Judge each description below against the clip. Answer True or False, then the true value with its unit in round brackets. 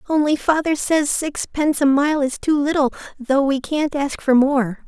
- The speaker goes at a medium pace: True (185 wpm)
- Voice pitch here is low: False (285 Hz)